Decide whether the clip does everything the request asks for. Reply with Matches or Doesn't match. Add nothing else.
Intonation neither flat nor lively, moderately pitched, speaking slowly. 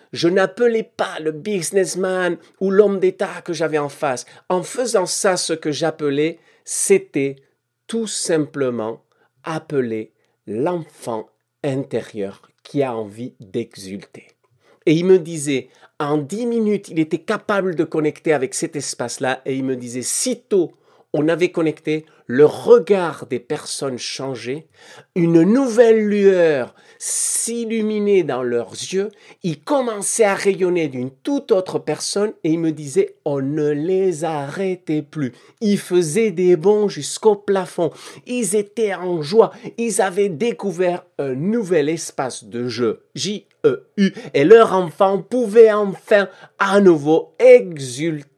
Doesn't match